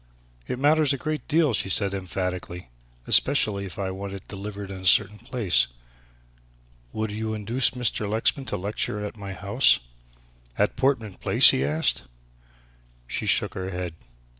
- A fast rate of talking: No, average, 155 wpm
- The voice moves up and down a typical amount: Yes, average, 4.1 semitones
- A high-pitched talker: No, low, 105 Hz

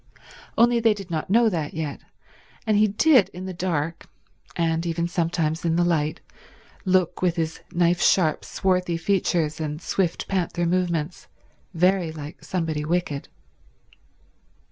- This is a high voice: No, medium, 175 Hz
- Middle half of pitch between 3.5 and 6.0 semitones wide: No, narrow, 2.5 semitones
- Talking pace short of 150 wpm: Yes, average, 140 wpm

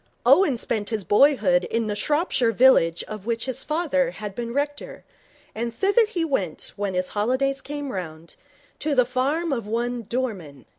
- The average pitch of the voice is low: No, high, 240 Hz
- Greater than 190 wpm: No, average, 165 wpm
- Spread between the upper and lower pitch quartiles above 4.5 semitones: Yes, average, 5.3 semitones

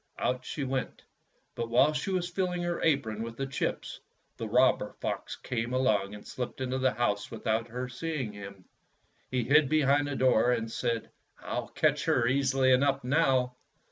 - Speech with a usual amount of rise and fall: Yes, average, 3.3 semitones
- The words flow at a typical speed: Yes, average, 170 wpm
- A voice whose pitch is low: Yes, low, 130 Hz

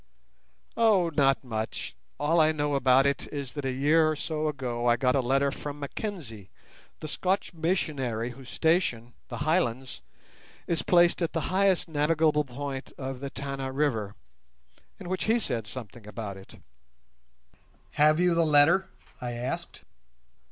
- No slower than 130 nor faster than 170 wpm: Yes, average, 150 wpm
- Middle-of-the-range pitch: Yes, medium, 145 Hz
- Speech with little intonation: No, average, 4.3 semitones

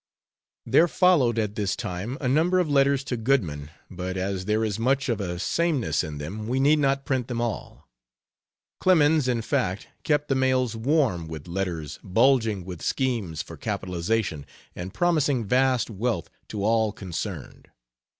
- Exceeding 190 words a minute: No, average, 160 wpm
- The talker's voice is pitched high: No, low, 115 Hz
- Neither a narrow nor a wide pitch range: No, wide, 6.5 semitones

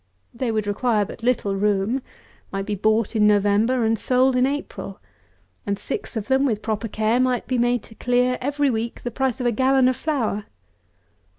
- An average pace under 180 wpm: No, average, 190 wpm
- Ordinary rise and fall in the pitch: Yes, average, 3.3 semitones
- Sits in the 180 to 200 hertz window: No, high, 235 Hz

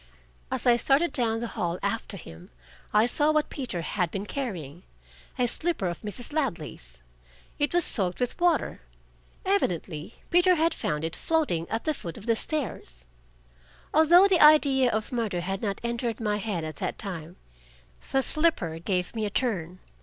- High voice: Yes, high, 225 Hz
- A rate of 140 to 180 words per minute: Yes, average, 170 wpm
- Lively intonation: Yes, wide, 8.7 semitones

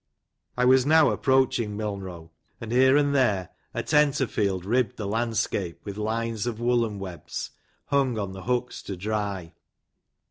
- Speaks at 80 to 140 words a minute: No, average, 150 wpm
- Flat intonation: No, average, 4.3 semitones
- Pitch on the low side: Yes, low, 110 Hz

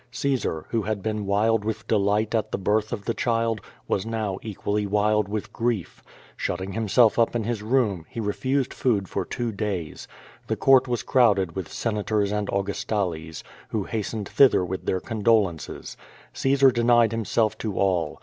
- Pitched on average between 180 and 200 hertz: No, low, 105 Hz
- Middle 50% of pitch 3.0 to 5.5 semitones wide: No, narrow, 2.6 semitones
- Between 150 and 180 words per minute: Yes, average, 175 wpm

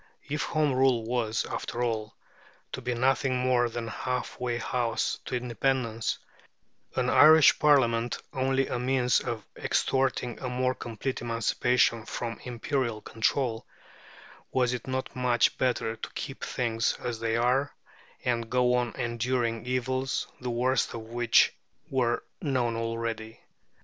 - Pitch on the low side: Yes, low, 125 Hz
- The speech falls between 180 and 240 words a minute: No, average, 140 wpm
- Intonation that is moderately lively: No, narrow, 1.9 semitones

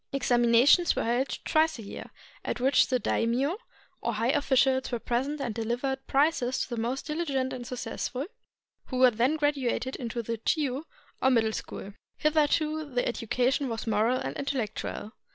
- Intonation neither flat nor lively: Yes, average, 3.1 semitones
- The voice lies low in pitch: No, very high, 255 Hz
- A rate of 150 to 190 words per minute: Yes, average, 160 wpm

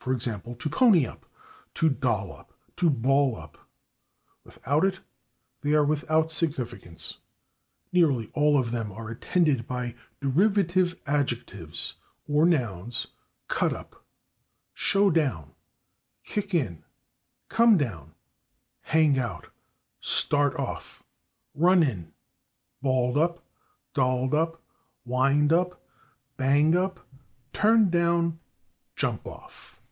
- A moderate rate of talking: No, slow, 105 wpm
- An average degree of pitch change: No, wide, 5.7 semitones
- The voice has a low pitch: No, medium, 145 Hz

